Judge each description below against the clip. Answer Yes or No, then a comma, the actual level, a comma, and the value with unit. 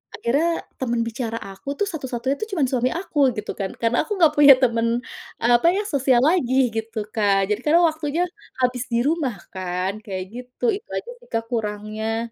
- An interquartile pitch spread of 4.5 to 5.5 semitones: Yes, average, 4.9 semitones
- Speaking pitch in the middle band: No, high, 245 Hz